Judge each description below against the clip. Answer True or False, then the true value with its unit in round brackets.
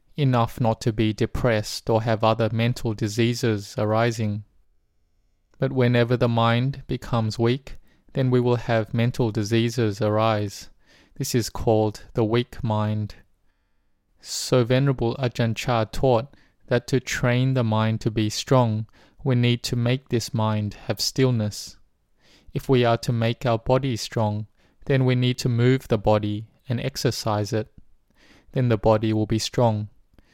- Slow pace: False (150 wpm)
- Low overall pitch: True (115 Hz)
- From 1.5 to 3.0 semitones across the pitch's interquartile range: True (2.6 semitones)